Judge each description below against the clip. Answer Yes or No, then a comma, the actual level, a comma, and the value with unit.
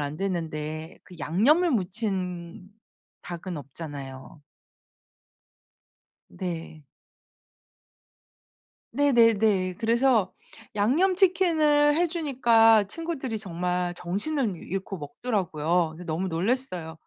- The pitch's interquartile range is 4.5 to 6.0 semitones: No, wide, 7.0 semitones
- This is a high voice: Yes, high, 195 Hz